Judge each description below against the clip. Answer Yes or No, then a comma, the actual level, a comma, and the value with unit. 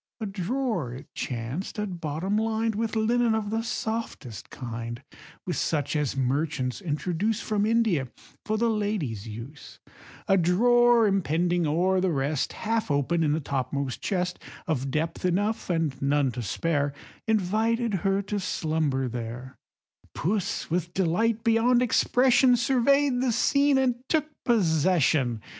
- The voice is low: No, medium, 180 Hz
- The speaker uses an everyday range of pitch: No, wide, 7.6 semitones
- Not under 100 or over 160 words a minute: Yes, average, 140 wpm